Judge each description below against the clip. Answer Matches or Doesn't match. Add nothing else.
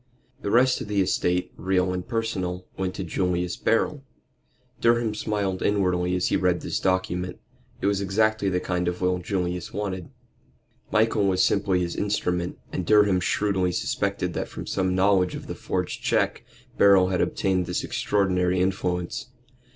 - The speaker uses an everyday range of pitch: Doesn't match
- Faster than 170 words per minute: Doesn't match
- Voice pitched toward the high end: Doesn't match